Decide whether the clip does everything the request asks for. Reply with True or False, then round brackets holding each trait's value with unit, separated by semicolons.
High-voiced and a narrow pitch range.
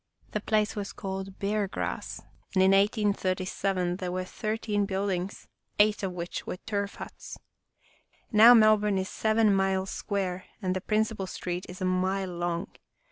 True (195 Hz; 2.3 semitones)